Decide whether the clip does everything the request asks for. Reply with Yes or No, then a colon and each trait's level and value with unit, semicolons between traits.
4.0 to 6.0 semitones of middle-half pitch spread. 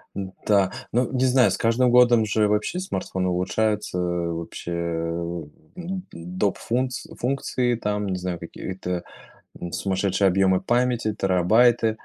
Yes: average, 5.1 semitones